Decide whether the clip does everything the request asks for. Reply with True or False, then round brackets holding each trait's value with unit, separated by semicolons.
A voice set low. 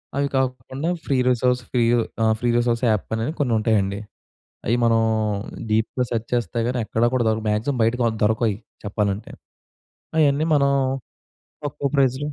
True (120 Hz)